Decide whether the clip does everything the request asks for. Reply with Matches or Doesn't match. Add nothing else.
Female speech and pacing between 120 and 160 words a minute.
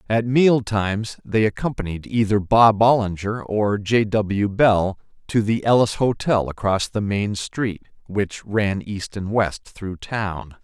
Doesn't match